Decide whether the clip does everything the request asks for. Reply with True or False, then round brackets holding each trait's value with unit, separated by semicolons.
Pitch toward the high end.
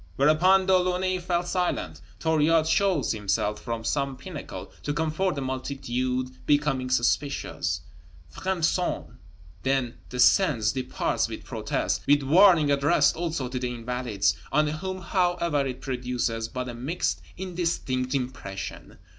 False (140 Hz)